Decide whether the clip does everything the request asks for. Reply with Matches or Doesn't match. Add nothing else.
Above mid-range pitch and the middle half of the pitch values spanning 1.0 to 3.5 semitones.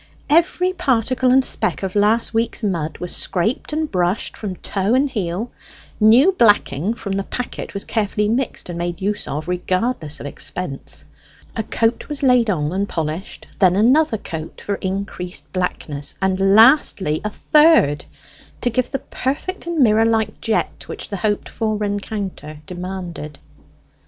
Doesn't match